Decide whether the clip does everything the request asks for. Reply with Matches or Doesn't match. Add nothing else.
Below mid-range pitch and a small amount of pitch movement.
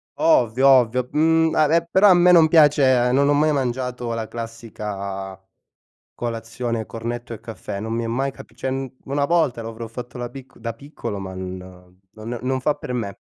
Doesn't match